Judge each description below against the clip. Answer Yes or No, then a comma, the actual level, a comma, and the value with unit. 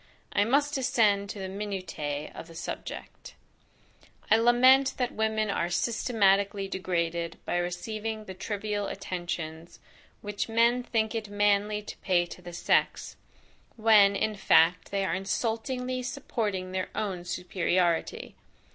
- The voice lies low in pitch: No, high, 200 Hz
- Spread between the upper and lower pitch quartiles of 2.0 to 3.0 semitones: No, average, 3.7 semitones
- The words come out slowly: Yes, slow, 130 wpm